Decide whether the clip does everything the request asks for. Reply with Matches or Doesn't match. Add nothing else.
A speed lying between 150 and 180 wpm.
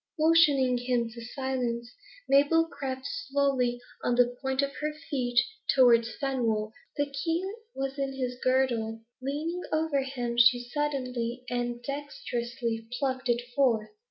Doesn't match